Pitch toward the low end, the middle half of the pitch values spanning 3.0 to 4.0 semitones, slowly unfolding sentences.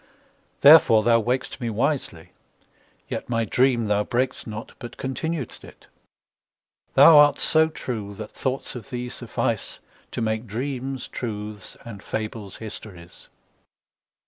Yes: low, 120 Hz; average, 3.6 semitones; slow, 115 wpm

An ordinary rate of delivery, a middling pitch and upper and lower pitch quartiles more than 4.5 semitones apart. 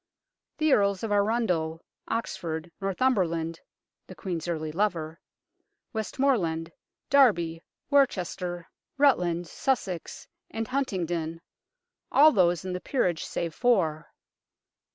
No: slow, 95 wpm; medium, 180 Hz; wide, 5.5 semitones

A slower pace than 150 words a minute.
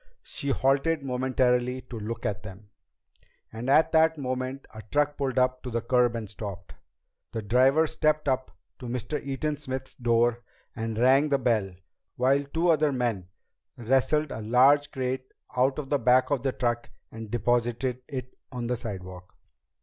No: average, 165 wpm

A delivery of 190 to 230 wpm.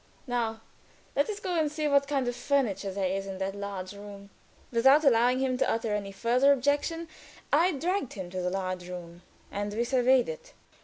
Yes: average, 195 wpm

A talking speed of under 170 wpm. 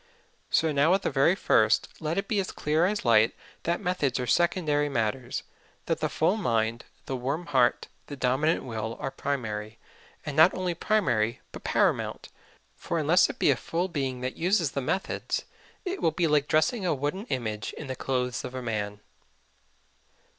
No: average, 180 wpm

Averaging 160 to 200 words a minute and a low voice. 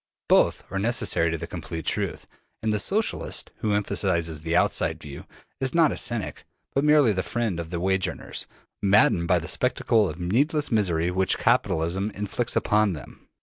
Yes: average, 180 wpm; low, 100 Hz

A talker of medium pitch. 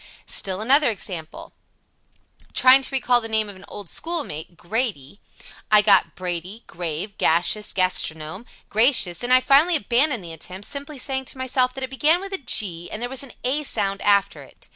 No: high, 220 Hz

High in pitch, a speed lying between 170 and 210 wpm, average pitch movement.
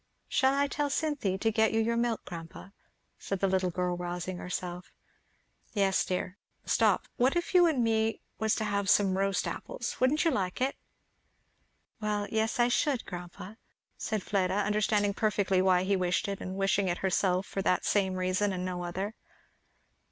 Yes: high, 200 Hz; average, 175 wpm; average, 3.3 semitones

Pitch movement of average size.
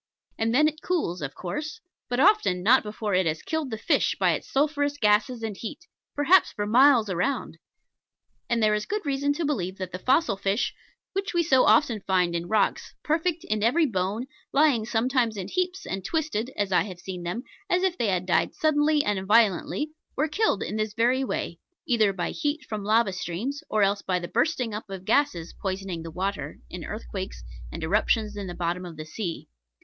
No: wide, 7.3 semitones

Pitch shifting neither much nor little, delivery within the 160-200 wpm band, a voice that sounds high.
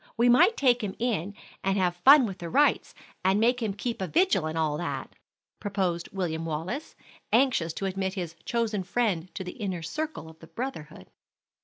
No: wide, 5.7 semitones; average, 185 wpm; high, 195 Hz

